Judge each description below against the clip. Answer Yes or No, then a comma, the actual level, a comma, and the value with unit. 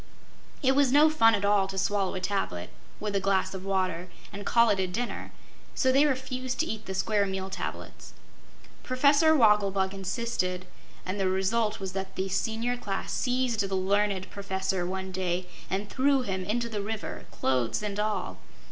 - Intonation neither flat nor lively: Yes, average, 3.6 semitones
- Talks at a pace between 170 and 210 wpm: Yes, average, 175 wpm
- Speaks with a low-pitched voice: No, high, 200 Hz